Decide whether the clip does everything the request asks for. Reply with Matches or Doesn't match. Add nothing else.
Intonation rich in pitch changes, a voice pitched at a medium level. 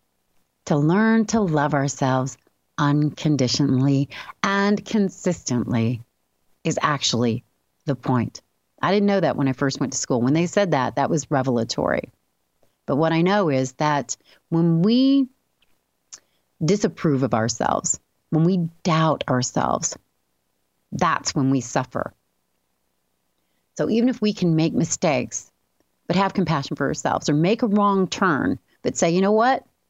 Matches